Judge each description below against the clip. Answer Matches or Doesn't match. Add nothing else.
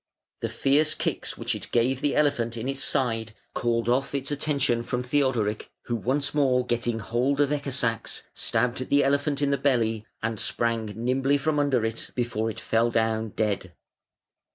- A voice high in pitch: Doesn't match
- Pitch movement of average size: Matches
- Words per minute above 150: Matches